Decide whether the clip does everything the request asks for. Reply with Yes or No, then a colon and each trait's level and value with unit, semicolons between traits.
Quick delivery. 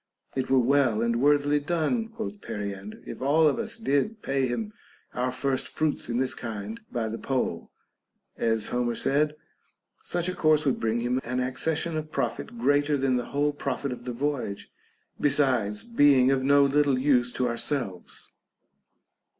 No: average, 165 wpm